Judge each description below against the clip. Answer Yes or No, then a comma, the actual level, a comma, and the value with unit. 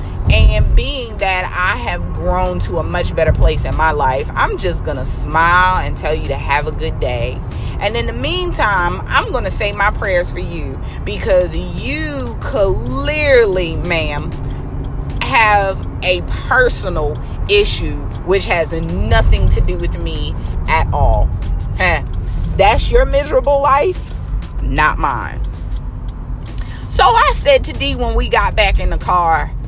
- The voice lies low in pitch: No, medium, 170 Hz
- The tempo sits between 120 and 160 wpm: Yes, average, 150 wpm